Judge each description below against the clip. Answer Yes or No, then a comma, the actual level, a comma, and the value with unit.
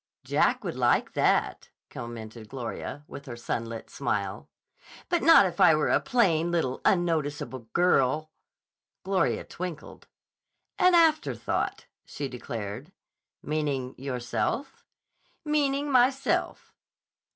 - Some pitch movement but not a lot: No, wide, 8.2 semitones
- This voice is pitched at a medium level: Yes, medium, 155 Hz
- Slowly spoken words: Yes, slow, 105 wpm